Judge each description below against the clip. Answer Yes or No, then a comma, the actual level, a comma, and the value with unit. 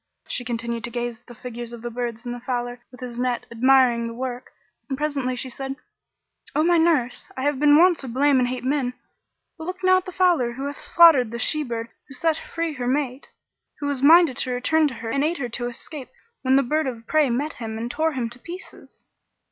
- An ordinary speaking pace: No, fast, 235 wpm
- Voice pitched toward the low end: No, very high, 255 Hz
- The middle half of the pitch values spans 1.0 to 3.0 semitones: No, average, 3.7 semitones